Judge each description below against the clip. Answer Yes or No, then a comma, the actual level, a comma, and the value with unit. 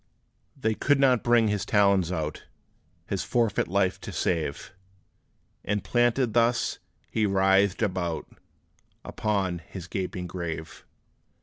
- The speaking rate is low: Yes, slow, 115 wpm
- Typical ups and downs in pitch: Yes, average, 3.7 semitones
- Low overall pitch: Yes, low, 100 Hz